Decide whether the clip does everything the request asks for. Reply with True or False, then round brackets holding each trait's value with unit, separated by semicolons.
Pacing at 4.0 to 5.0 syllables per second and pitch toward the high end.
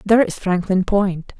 True (4.7 syllables/s; 195 Hz)